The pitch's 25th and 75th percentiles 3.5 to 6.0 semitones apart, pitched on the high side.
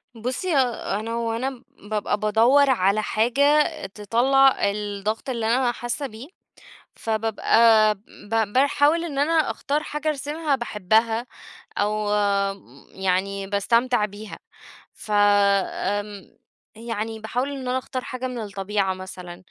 Yes: average, 4.0 semitones; high, 225 Hz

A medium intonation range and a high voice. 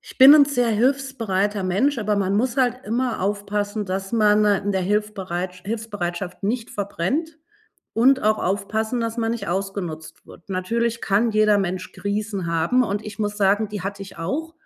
Yes: average, 3.1 semitones; high, 210 Hz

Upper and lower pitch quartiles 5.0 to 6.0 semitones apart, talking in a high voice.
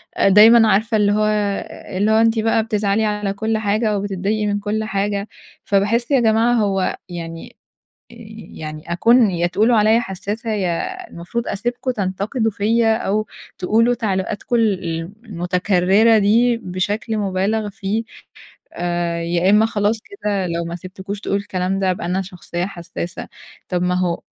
No: average, 3.0 semitones; high, 205 Hz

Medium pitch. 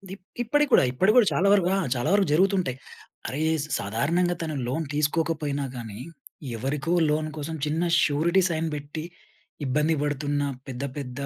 Yes: medium, 155 Hz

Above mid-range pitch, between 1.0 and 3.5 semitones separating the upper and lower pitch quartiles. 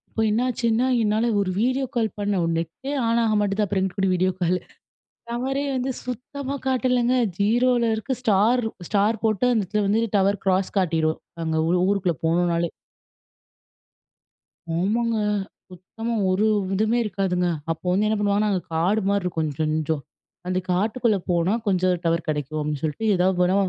No: high, 200 Hz; average, 4.2 semitones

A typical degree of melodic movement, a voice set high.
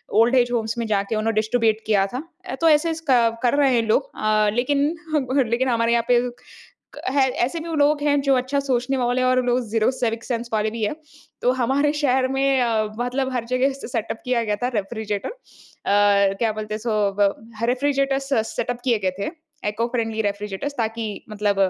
Yes: average, 3.3 semitones; high, 240 Hz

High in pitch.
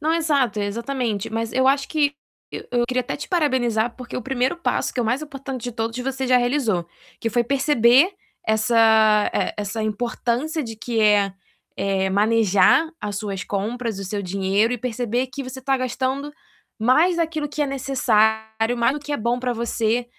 Yes: high, 240 Hz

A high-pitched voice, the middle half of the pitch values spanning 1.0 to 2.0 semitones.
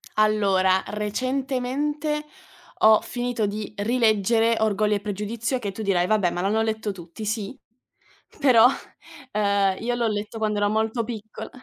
No: high, 215 Hz; average, 2.8 semitones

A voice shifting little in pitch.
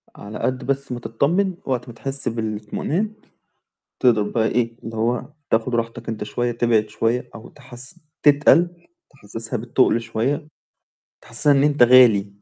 No: average, 3.5 semitones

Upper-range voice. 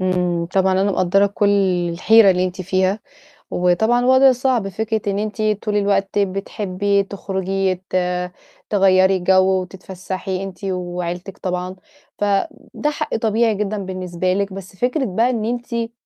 Yes: high, 195 Hz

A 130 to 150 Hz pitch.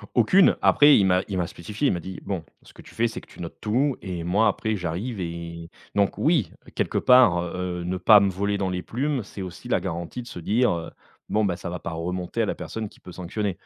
No: very low, 95 Hz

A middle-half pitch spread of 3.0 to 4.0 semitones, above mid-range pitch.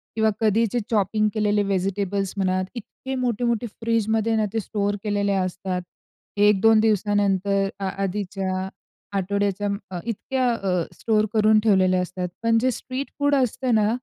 No: narrow, 2.5 semitones; high, 205 Hz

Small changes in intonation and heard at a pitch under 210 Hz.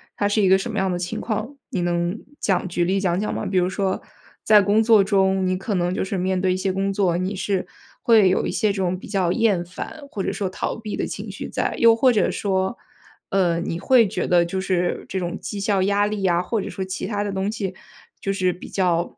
Yes: narrow, 2.0 semitones; high, 190 Hz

